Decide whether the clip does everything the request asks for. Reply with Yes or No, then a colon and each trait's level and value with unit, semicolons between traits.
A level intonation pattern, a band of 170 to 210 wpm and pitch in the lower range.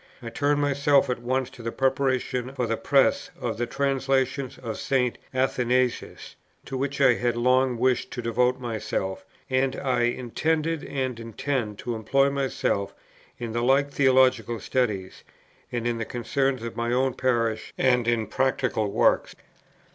No: narrow, 2.2 semitones; average, 155 wpm; low, 125 Hz